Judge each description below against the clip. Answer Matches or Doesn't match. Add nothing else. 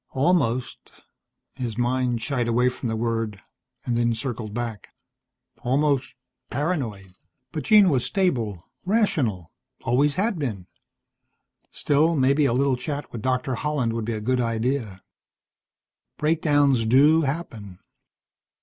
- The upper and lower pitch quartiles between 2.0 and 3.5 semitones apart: Doesn't match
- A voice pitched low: Matches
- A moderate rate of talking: Doesn't match